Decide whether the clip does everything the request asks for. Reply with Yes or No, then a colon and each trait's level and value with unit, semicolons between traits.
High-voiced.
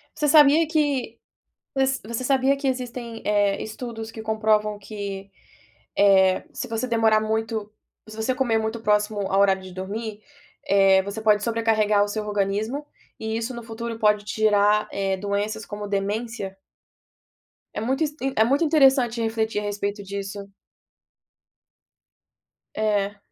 Yes: high, 220 Hz